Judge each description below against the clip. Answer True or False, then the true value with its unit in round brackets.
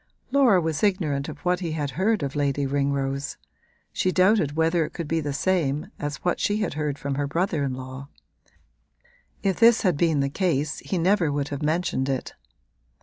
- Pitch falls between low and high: True (155 Hz)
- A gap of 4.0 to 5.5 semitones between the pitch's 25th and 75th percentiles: True (4.5 semitones)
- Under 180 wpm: False (190 wpm)